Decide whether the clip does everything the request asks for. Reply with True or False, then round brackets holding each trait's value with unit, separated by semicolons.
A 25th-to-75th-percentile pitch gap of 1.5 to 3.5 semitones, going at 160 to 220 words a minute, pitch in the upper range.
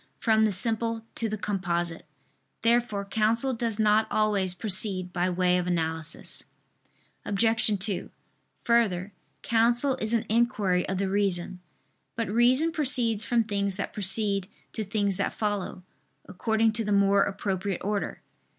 False (3.1 semitones; 140 wpm; 205 Hz)